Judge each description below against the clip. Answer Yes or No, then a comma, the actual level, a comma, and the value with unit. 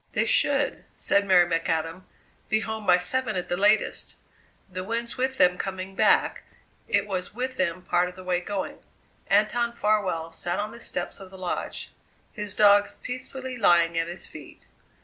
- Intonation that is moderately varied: Yes, average, 3.3 semitones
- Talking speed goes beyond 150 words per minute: Yes, average, 170 wpm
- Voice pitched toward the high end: Yes, high, 195 Hz